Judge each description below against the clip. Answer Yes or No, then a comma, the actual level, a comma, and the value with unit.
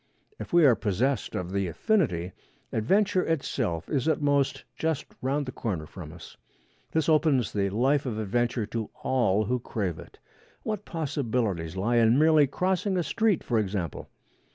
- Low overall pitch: Yes, low, 125 Hz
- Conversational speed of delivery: Yes, average, 160 wpm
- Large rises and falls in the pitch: Yes, wide, 7.1 semitones